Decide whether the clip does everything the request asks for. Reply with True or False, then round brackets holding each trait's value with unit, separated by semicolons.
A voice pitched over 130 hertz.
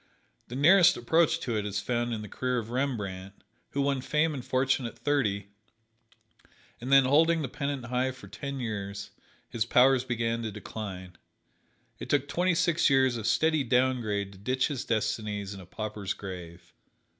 False (120 Hz)